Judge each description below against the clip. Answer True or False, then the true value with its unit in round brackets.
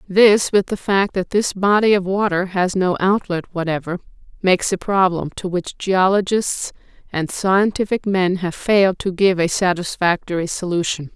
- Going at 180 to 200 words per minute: False (155 wpm)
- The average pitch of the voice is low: False (185 Hz)